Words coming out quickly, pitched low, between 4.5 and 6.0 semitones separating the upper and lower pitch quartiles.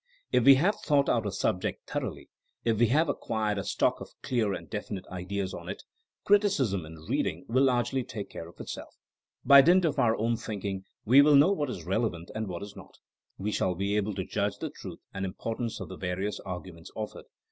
Yes: fast, 210 wpm; low, 105 Hz; average, 5.1 semitones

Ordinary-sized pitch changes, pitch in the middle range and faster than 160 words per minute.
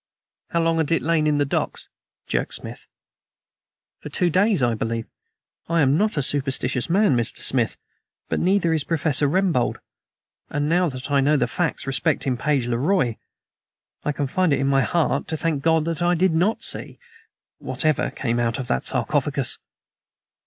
Yes: average, 3.9 semitones; medium, 150 Hz; average, 175 wpm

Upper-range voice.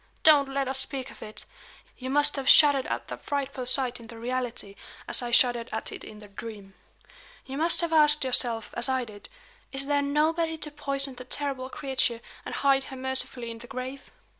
Yes: very high, 265 Hz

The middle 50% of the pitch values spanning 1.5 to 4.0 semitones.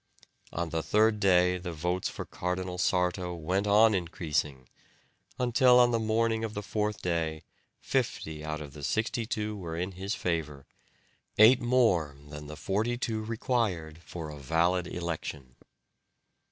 No: average, 5.3 semitones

